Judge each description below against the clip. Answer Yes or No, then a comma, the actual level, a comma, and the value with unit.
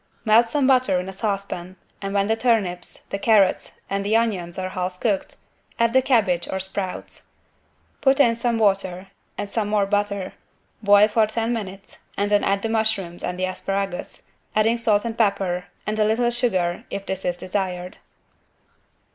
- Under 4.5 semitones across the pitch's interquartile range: Yes, average, 3.1 semitones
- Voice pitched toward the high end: Yes, high, 200 Hz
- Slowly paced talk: No, average, 170 wpm